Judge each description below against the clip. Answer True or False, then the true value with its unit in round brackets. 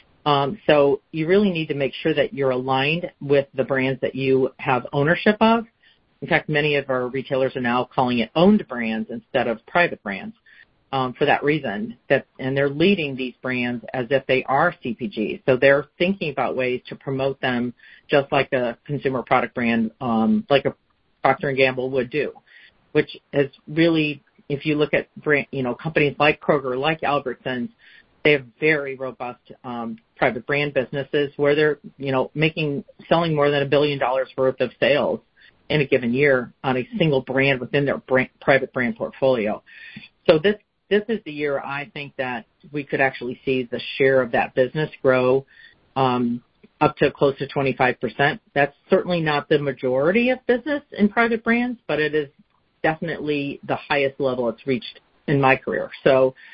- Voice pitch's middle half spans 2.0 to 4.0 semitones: True (2.8 semitones)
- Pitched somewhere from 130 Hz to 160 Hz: True (140 Hz)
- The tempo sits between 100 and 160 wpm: False (185 wpm)